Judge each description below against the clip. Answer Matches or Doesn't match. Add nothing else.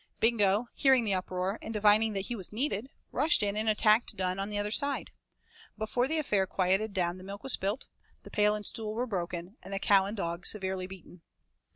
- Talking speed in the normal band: Doesn't match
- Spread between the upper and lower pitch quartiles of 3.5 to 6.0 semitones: Doesn't match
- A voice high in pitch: Matches